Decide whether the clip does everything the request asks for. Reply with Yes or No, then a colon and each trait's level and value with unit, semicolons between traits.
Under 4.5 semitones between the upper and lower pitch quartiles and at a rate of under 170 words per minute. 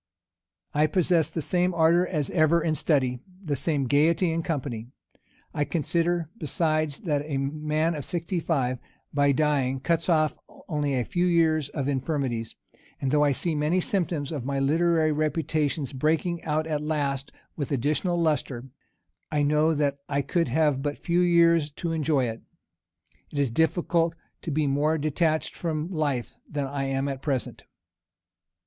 Yes: average, 2.8 semitones; average, 160 wpm